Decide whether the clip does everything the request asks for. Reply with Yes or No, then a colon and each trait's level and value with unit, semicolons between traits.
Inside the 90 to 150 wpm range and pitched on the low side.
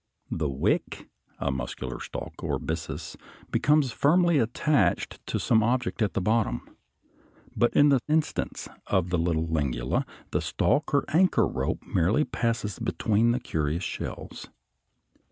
Yes: slow, 135 wpm; low, 110 Hz